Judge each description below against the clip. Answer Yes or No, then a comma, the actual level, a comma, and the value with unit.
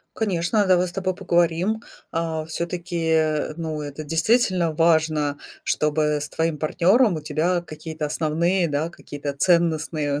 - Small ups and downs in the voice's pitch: Yes, narrow, 2.3 semitones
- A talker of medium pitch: Yes, medium, 165 Hz